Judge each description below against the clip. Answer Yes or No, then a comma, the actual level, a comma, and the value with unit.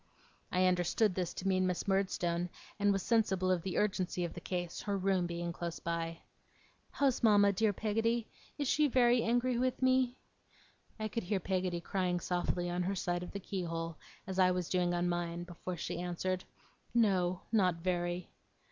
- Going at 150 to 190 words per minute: Yes, average, 175 wpm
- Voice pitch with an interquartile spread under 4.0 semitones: Yes, average, 2.8 semitones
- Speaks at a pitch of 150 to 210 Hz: Yes, medium, 185 Hz